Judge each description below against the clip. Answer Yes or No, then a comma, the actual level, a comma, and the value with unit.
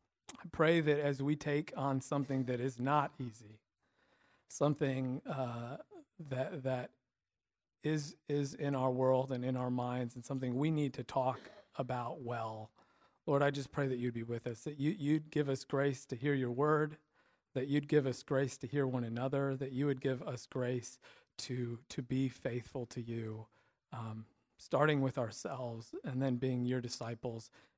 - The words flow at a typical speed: Yes, average, 175 wpm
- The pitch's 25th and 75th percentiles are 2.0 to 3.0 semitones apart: Yes, narrow, 2.6 semitones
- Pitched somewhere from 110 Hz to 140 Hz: Yes, low, 130 Hz